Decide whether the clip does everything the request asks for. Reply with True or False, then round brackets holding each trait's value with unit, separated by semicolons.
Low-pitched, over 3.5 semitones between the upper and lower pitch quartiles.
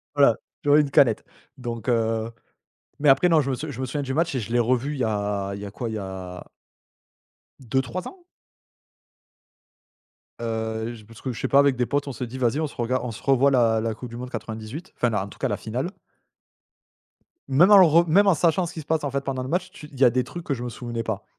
True (125 Hz; 4.2 semitones)